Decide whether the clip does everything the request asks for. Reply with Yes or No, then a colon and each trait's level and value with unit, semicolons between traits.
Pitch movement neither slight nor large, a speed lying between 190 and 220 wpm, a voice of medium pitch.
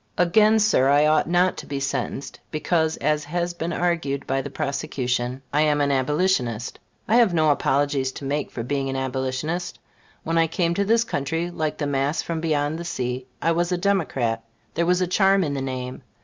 Yes: average, 4.2 semitones; average, 200 wpm; medium, 150 Hz